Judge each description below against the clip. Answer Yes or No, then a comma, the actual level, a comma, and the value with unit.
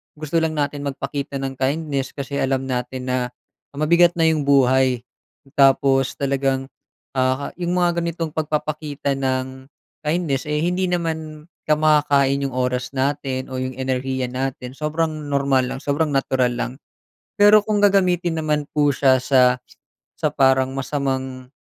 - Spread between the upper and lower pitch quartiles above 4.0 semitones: No, average, 2.8 semitones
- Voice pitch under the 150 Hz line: Yes, medium, 140 Hz